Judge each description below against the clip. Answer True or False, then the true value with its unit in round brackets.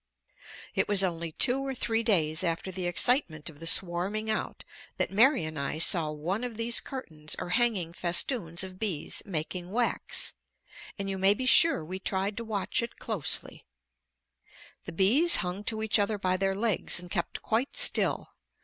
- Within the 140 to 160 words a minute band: False (175 wpm)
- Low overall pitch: False (195 Hz)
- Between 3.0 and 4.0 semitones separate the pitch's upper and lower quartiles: False (4.7 semitones)